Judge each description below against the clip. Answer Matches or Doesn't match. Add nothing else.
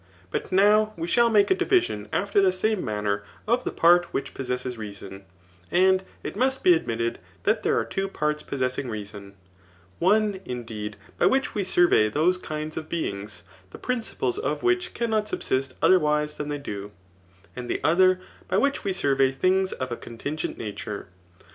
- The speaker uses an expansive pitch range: Matches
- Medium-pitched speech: Matches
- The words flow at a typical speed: Matches